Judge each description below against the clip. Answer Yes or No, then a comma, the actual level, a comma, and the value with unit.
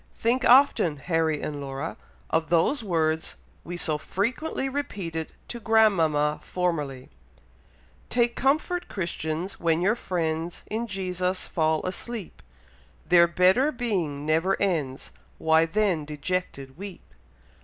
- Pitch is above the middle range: No, medium, 175 Hz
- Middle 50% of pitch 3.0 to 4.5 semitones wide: No, average, 5.2 semitones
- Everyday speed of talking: No, slow, 115 wpm